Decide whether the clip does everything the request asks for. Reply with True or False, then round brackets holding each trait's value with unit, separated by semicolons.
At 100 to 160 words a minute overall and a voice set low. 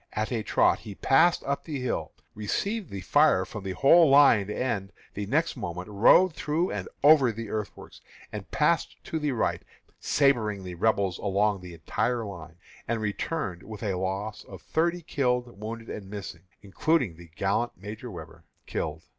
False (170 wpm; 110 Hz)